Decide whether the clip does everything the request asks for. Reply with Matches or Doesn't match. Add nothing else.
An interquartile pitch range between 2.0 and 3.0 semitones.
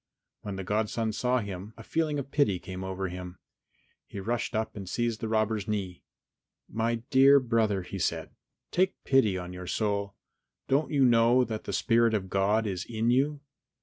Doesn't match